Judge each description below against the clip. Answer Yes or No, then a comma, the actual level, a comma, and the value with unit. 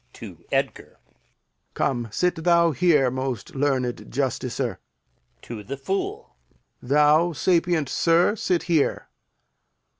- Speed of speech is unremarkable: No, slow, 100 wpm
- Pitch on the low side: No, medium, 145 Hz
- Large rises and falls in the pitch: No, average, 4.8 semitones